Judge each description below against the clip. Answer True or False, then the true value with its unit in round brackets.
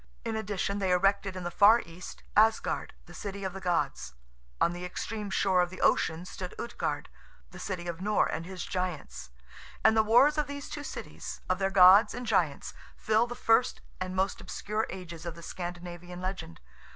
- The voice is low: False (190 Hz)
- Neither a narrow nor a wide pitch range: True (3.3 semitones)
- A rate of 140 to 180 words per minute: False (190 wpm)